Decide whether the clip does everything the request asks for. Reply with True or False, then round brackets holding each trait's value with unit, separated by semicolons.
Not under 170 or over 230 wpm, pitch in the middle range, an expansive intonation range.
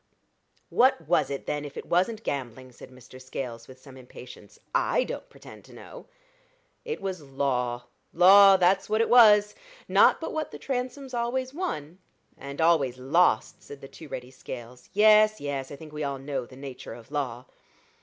True (175 wpm; 145 Hz; 8.1 semitones)